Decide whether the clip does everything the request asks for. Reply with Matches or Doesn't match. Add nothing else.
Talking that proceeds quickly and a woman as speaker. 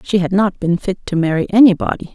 Matches